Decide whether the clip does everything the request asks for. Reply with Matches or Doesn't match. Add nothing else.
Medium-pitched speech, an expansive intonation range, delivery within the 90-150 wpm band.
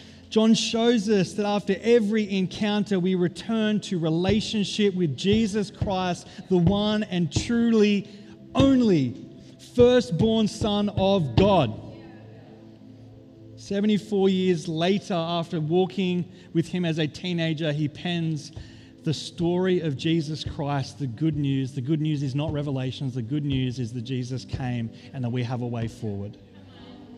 Matches